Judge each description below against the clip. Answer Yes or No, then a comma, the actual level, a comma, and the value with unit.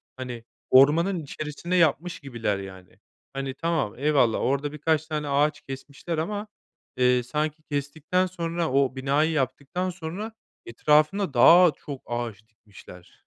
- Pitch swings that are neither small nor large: Yes, average, 4.0 semitones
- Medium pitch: Yes, medium, 145 Hz